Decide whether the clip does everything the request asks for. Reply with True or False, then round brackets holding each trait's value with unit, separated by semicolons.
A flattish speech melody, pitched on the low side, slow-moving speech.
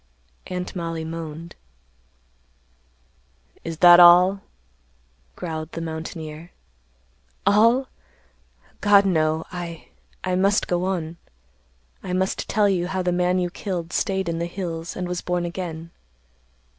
False (2.1 semitones; 175 Hz; 120 wpm)